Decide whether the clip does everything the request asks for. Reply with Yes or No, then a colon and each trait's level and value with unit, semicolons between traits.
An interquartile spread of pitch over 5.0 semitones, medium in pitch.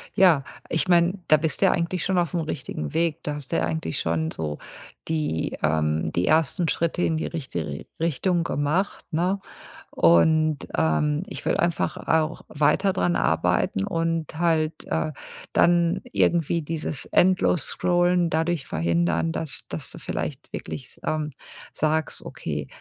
Yes: wide, 5.5 semitones; medium, 155 Hz